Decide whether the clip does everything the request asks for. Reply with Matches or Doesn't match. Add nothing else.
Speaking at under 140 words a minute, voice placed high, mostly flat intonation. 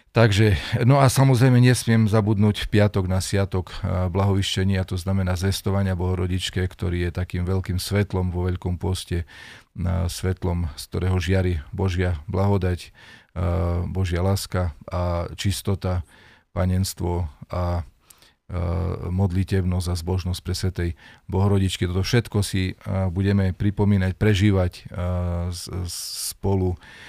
Doesn't match